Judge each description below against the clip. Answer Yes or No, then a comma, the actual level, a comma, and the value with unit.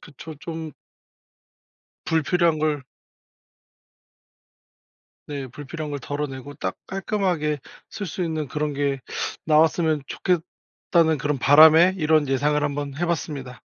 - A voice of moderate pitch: Yes, medium, 150 Hz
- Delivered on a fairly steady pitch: Yes, narrow, 2.2 semitones